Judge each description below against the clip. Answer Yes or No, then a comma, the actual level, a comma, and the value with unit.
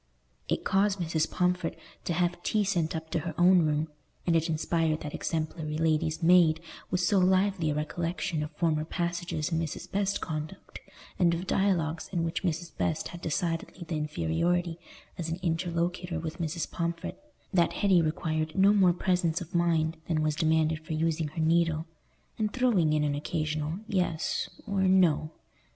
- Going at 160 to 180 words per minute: Yes, average, 170 wpm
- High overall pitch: No, medium, 165 Hz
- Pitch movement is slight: Yes, narrow, 2.2 semitones